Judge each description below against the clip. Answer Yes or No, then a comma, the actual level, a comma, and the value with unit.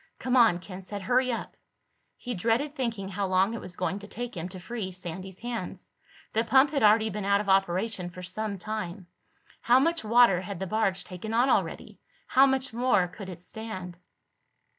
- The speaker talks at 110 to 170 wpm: No, average, 190 wpm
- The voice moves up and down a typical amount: Yes, average, 4.3 semitones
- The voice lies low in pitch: No, high, 210 Hz